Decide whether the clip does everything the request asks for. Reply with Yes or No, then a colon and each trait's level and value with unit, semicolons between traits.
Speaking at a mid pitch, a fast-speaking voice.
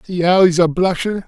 Yes: medium, 180 Hz; fast, 235 wpm